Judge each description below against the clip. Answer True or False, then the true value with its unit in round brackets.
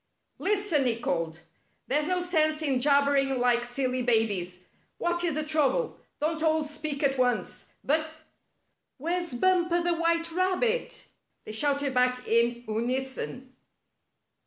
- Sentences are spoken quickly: False (150 wpm)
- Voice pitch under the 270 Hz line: False (285 Hz)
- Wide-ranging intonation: False (5.0 semitones)